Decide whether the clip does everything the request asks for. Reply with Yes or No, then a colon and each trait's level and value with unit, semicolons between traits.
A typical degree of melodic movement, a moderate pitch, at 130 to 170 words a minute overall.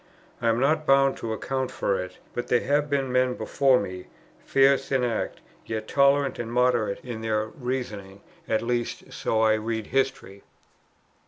No: average, 3.5 semitones; low, 120 Hz; average, 165 wpm